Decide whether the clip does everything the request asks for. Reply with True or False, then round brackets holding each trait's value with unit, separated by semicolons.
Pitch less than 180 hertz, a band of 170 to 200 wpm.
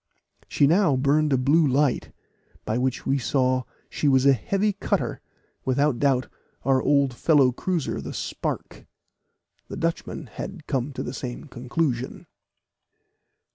False (135 Hz; 135 wpm)